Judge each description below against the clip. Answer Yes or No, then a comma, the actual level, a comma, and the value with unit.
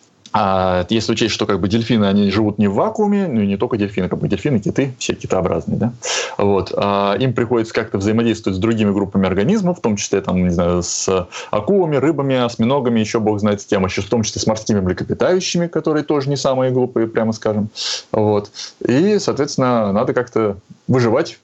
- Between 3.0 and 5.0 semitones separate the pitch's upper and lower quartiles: Yes, average, 4.2 semitones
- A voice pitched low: Yes, low, 110 Hz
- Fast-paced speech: Yes, fast, 195 wpm